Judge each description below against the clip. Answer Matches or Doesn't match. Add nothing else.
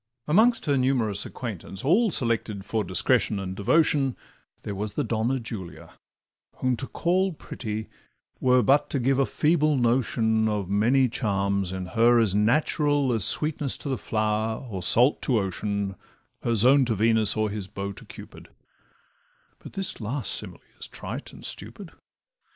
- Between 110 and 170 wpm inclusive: Matches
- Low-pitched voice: Matches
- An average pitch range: Matches